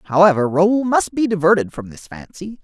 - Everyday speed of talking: Yes, average, 180 wpm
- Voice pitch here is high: No, medium, 180 Hz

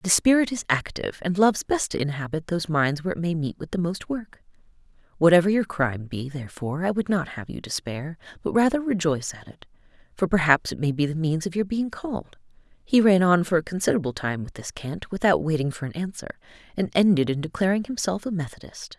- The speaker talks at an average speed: No, fast, 215 wpm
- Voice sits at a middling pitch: Yes, medium, 170 Hz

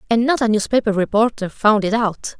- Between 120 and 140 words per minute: No, average, 200 wpm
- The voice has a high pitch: Yes, high, 220 Hz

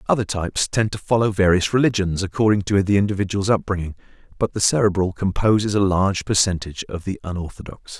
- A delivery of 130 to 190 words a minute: Yes, average, 150 wpm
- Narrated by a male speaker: Yes, male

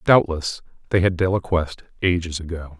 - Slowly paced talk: Yes, slow, 130 wpm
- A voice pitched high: No, very low, 85 Hz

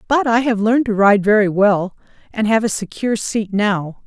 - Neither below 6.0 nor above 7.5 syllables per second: No, 5.1 syllables/s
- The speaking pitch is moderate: No, high, 210 Hz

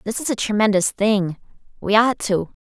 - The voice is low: No, high, 205 Hz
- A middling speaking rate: Yes, average, 180 wpm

